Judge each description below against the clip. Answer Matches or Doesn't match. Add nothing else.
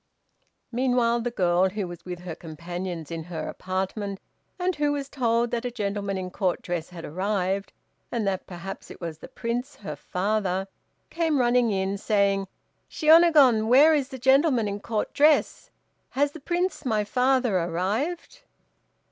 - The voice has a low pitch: Doesn't match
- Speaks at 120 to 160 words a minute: Matches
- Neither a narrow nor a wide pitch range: Doesn't match